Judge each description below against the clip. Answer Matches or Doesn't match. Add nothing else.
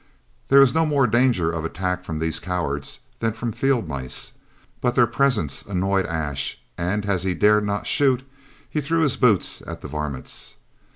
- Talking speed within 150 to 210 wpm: Matches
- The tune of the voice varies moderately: Doesn't match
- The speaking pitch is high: Doesn't match